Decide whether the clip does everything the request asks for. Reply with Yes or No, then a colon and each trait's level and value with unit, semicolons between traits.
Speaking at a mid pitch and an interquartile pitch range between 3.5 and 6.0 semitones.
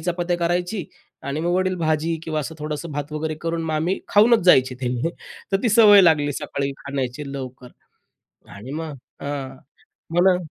Yes: medium, 155 Hz; average, 3.9 semitones